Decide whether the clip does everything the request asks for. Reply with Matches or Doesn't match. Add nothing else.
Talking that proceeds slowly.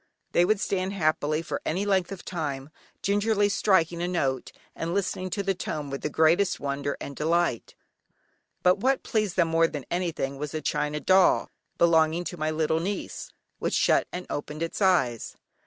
Doesn't match